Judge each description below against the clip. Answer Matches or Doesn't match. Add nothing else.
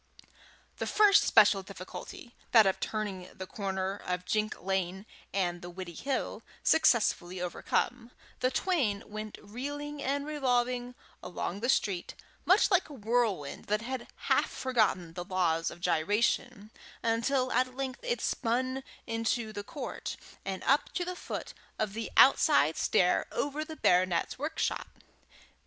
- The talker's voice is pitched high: Matches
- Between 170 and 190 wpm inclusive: Doesn't match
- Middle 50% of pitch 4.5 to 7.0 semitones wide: Matches